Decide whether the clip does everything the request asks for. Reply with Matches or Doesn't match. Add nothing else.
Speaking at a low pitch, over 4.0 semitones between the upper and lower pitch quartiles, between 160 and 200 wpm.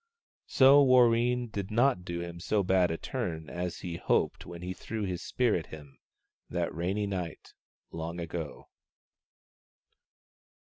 Doesn't match